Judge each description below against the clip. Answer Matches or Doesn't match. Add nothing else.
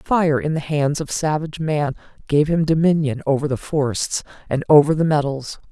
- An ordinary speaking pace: Matches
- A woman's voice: Matches